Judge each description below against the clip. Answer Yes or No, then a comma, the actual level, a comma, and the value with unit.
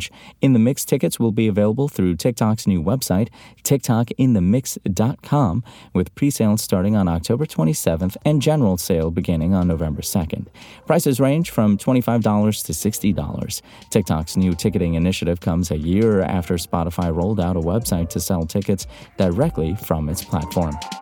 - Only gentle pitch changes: No, average, 4.8 semitones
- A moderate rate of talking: Yes, average, 145 wpm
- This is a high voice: No, low, 100 Hz